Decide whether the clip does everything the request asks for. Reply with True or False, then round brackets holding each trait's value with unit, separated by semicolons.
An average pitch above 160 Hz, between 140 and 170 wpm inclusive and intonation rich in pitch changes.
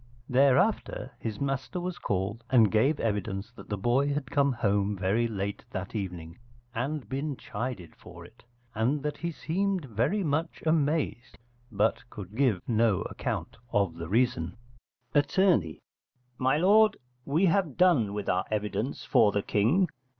False (120 Hz; 150 wpm; 6.2 semitones)